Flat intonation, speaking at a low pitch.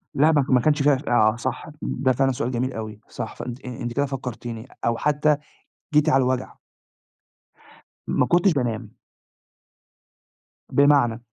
No: average, 3.2 semitones; low, 130 Hz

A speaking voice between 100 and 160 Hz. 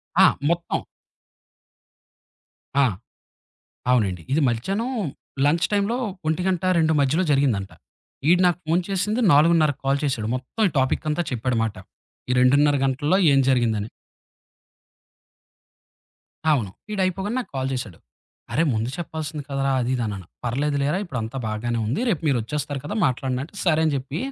Yes: medium, 140 Hz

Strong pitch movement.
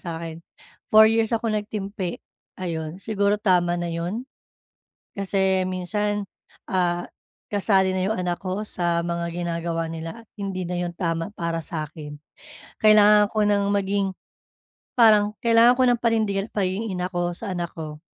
No: average, 3.3 semitones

